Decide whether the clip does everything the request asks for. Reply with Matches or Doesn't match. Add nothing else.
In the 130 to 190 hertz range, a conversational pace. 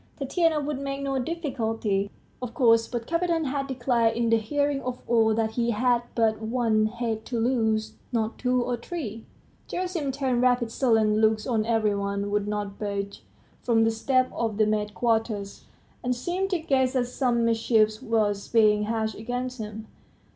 Doesn't match